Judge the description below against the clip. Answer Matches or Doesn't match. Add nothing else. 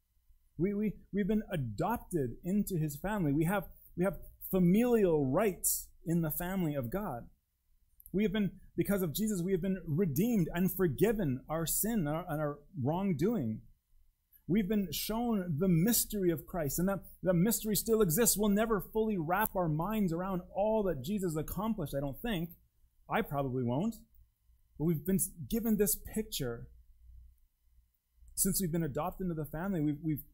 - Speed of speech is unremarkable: Matches